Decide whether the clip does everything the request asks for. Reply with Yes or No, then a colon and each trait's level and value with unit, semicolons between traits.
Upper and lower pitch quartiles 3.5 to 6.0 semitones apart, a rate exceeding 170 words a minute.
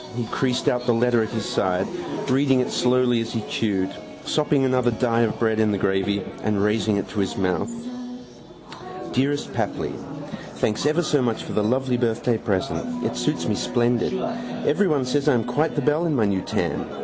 Yes: average, 3.8 semitones; average, 190 wpm